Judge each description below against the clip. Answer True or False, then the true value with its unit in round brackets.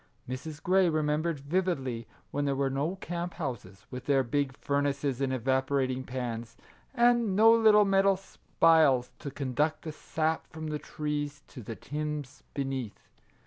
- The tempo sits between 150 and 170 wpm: True (155 wpm)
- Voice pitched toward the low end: False (145 Hz)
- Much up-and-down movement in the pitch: False (3.8 semitones)